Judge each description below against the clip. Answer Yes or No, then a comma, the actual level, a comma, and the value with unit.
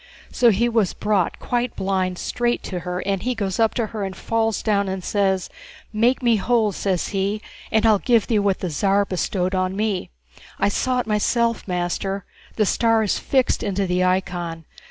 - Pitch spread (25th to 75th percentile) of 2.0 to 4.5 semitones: Yes, average, 3.2 semitones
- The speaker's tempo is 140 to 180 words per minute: No, average, 190 wpm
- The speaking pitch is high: Yes, high, 200 Hz